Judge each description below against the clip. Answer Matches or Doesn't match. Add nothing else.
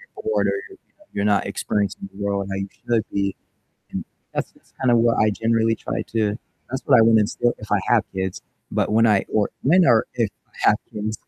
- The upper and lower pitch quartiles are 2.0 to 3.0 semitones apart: Matches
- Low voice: Matches